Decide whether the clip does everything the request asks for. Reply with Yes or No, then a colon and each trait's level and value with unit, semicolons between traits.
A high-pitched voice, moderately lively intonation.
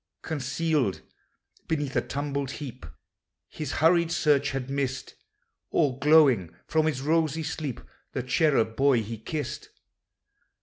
No: medium, 140 Hz; average, 3.3 semitones